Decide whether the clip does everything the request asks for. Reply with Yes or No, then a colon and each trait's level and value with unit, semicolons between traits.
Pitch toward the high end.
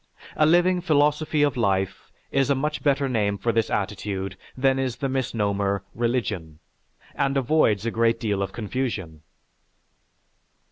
No: low, 120 Hz